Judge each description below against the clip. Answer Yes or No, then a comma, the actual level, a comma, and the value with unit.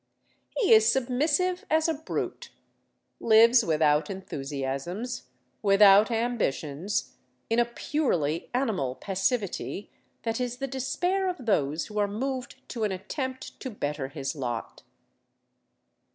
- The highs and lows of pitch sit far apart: Yes, wide, 8.0 semitones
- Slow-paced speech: Yes, slow, 120 wpm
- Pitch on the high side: Yes, high, 220 Hz